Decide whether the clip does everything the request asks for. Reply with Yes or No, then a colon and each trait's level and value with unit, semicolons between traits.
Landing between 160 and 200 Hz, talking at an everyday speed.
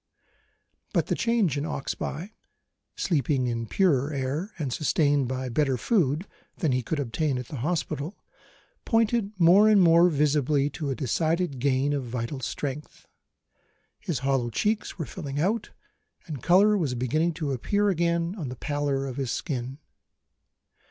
No: medium, 145 Hz; average, 150 wpm